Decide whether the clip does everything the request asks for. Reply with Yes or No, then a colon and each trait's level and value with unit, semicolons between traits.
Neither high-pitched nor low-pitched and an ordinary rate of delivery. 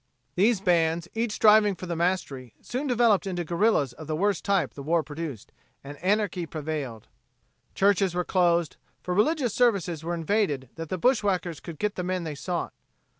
Yes: medium, 180 Hz; average, 175 wpm